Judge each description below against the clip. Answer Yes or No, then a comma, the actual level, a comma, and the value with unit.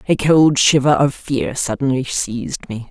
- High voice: No, low, 130 Hz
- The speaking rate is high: No, average, 165 wpm